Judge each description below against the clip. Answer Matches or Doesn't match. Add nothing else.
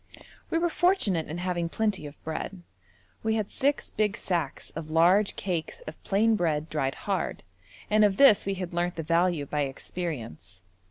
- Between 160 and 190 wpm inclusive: Matches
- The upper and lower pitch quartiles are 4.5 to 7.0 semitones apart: Matches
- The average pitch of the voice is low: Doesn't match